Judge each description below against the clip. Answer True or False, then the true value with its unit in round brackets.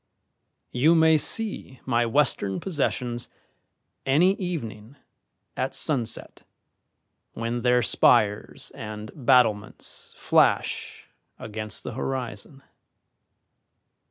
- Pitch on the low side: True (125 Hz)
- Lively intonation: False (5.0 semitones)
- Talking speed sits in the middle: False (80 wpm)